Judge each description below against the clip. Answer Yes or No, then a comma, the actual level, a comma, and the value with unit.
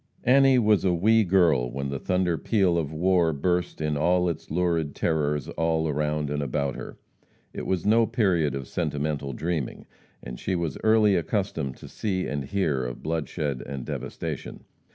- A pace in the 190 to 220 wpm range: No, average, 170 wpm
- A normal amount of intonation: Yes, average, 4.3 semitones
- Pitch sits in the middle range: No, very low, 80 Hz